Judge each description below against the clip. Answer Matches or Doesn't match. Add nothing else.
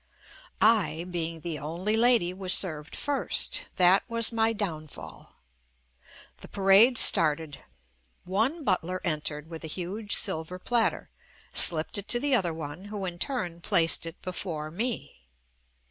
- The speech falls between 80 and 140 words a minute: Matches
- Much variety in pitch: Doesn't match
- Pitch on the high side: Doesn't match